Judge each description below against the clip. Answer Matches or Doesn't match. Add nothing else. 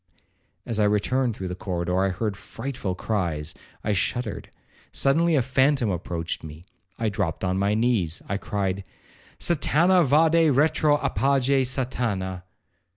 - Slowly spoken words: Matches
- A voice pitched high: Doesn't match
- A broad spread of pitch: Matches